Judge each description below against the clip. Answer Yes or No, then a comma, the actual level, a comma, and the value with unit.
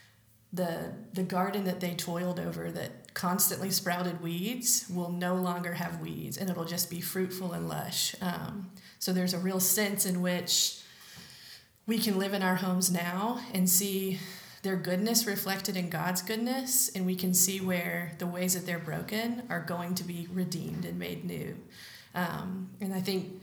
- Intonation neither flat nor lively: No, narrow, 1.5 semitones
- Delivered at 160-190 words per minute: Yes, average, 175 wpm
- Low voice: No, medium, 185 Hz